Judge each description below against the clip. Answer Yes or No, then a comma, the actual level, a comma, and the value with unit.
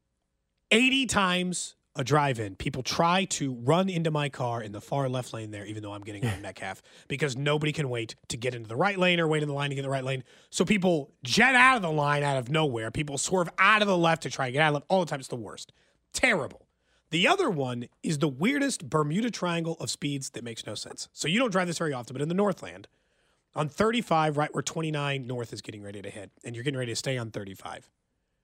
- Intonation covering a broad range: Yes, wide, 5.7 semitones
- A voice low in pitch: No, medium, 145 Hz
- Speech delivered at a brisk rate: Yes, fast, 255 wpm